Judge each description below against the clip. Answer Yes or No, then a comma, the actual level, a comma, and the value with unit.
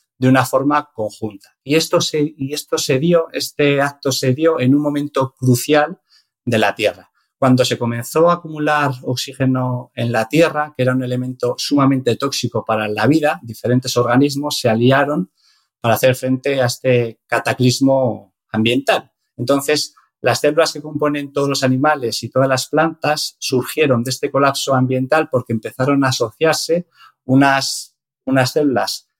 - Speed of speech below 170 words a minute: Yes, average, 155 wpm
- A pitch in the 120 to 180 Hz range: Yes, low, 135 Hz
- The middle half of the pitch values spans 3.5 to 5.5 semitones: No, average, 2.8 semitones